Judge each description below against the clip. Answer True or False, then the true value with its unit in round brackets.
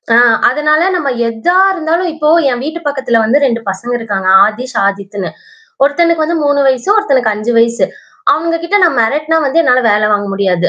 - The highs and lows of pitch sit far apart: True (6.3 semitones)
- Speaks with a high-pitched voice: True (260 Hz)